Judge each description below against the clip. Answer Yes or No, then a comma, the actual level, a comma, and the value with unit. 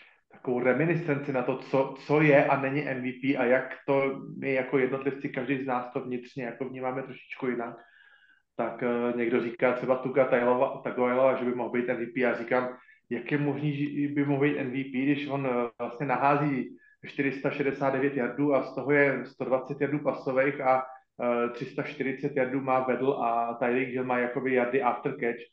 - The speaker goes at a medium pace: No, fast, 175 wpm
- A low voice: Yes, low, 130 Hz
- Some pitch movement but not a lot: No, narrow, 2.0 semitones